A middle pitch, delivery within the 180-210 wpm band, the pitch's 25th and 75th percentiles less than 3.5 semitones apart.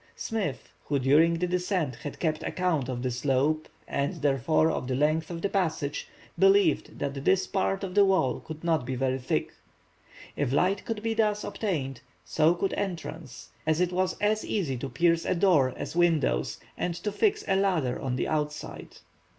No: medium, 160 Hz; average, 185 wpm; wide, 5.4 semitones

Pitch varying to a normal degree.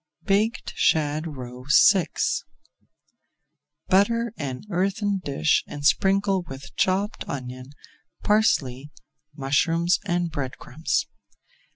No: wide, 6.1 semitones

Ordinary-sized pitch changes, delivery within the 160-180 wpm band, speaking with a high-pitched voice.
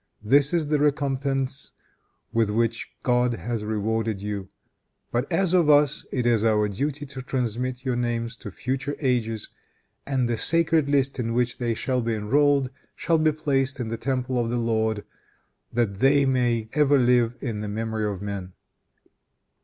No: average, 3.6 semitones; average, 165 wpm; low, 125 Hz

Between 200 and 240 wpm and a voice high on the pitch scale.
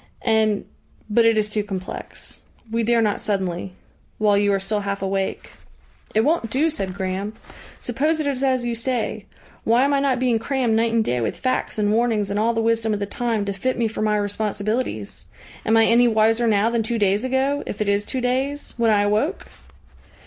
Yes: fast, 205 wpm; high, 220 Hz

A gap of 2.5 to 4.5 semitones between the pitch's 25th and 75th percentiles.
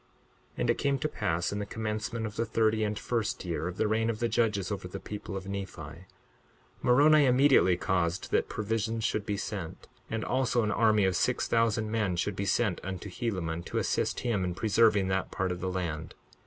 Yes: average, 3.4 semitones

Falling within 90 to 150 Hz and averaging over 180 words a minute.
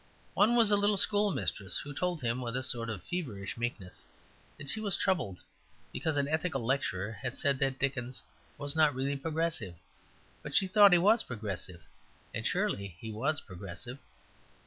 No: low, 135 Hz; average, 170 wpm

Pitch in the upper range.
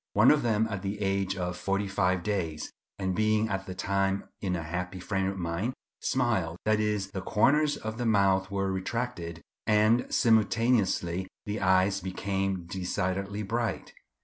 No: low, 100 Hz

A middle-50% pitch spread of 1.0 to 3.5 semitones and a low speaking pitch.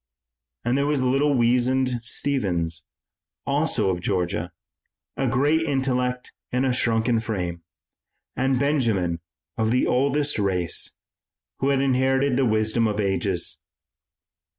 No: average, 4.5 semitones; low, 125 Hz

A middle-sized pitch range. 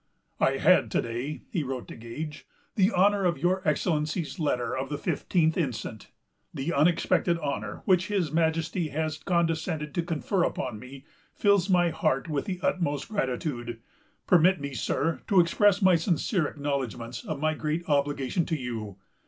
Yes: average, 4.2 semitones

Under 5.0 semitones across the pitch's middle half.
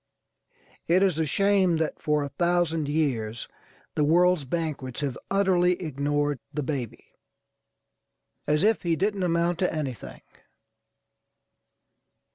Yes: average, 3.5 semitones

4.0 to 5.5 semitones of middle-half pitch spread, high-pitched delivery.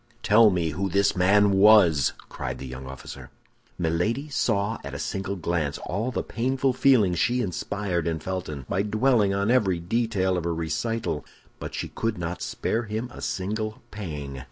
No: average, 4.7 semitones; low, 100 Hz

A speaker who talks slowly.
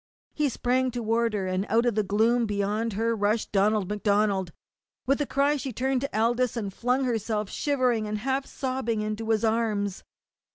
No: average, 175 wpm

